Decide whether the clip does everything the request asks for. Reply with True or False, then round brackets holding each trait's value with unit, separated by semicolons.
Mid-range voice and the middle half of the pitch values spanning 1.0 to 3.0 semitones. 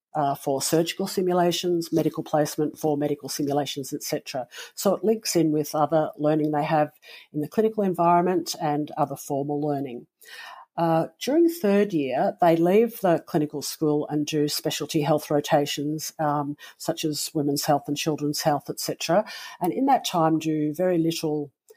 True (155 Hz; 2.4 semitones)